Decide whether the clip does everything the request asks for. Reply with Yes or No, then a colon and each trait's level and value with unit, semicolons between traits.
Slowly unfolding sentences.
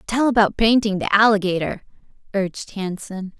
Yes: slow, 125 wpm